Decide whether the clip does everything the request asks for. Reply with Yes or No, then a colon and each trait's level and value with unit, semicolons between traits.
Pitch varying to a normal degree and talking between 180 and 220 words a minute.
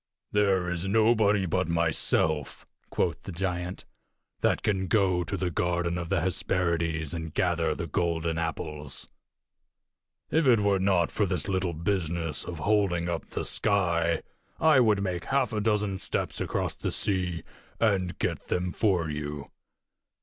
No: average, 3.1 semitones; average, 150 wpm